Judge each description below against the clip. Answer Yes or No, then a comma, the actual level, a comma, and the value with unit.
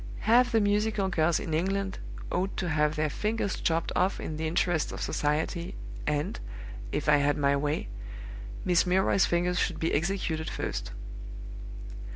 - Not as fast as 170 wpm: Yes, average, 155 wpm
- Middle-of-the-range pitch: Yes, medium, 170 Hz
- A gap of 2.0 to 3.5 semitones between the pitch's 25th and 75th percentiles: No, average, 4.1 semitones